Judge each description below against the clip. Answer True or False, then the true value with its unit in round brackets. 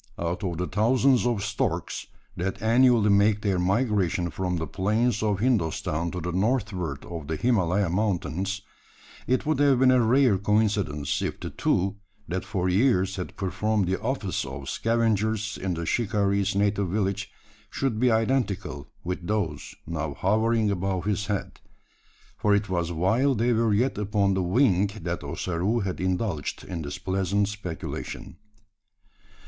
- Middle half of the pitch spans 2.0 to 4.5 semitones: True (3.6 semitones)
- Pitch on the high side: False (100 Hz)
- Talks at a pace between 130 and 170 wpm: True (155 wpm)